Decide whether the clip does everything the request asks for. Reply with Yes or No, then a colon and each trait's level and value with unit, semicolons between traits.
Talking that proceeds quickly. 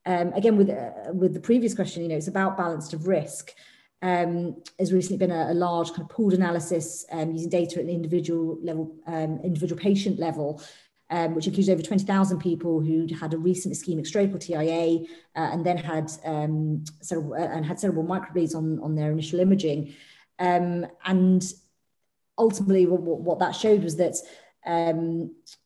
No: average, 180 wpm